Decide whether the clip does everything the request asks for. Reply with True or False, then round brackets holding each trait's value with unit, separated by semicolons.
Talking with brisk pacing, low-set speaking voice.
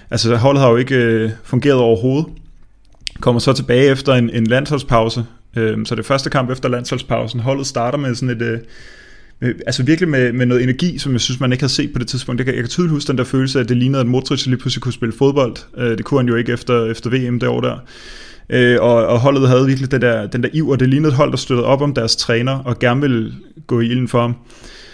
True (250 wpm; 125 Hz)